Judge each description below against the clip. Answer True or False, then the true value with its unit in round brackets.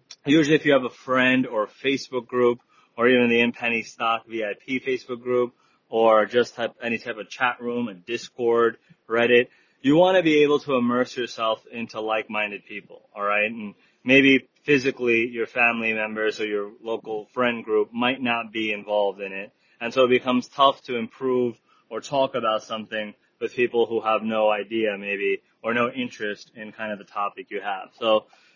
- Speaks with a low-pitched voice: True (115 Hz)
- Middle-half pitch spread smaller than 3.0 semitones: True (2.5 semitones)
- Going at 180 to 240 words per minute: True (185 wpm)